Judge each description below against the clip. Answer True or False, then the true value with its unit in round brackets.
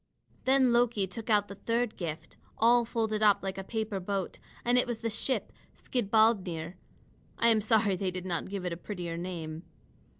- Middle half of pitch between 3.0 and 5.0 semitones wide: True (3.9 semitones)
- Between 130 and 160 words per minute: False (185 wpm)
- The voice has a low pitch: False (205 Hz)